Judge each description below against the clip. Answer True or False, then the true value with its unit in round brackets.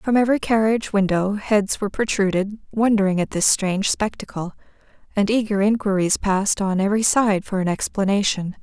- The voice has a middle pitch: False (205 Hz)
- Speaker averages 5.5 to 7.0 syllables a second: True (5.6 syllables/s)